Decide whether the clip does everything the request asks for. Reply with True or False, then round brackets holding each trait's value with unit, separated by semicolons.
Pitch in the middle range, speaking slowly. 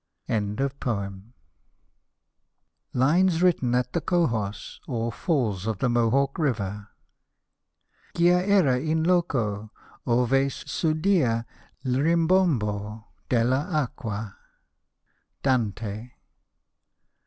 False (125 Hz; 85 wpm)